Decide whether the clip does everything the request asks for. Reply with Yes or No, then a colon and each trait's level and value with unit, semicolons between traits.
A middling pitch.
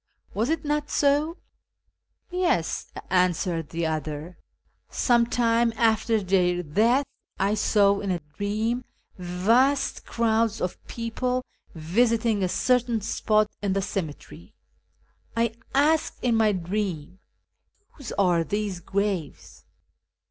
No: high, 215 Hz